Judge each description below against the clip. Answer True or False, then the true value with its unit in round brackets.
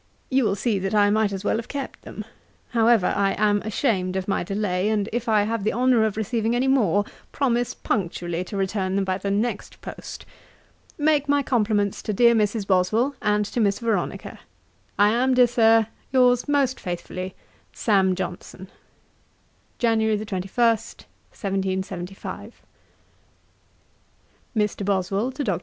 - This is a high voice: True (210 Hz)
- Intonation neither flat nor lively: True (3.4 semitones)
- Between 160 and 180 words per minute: False (150 wpm)